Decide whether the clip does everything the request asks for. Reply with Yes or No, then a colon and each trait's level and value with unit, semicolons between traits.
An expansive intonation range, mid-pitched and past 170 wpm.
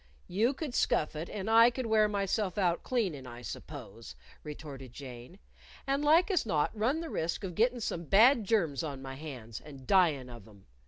Yes: wide, 8.6 semitones; medium, 180 Hz; average, 190 wpm